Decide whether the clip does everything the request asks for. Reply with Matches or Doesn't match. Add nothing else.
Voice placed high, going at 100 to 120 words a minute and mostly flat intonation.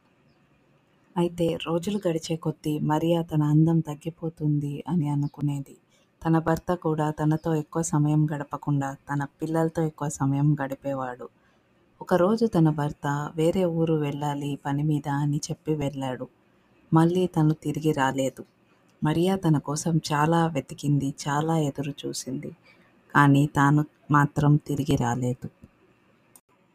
Doesn't match